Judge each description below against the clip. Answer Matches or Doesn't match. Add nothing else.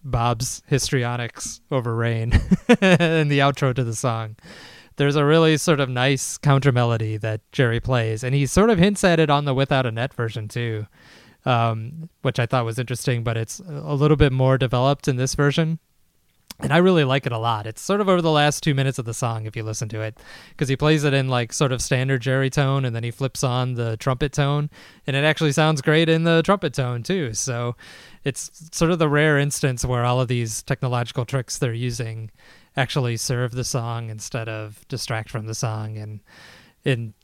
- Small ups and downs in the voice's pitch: Doesn't match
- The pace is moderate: Doesn't match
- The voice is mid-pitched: Doesn't match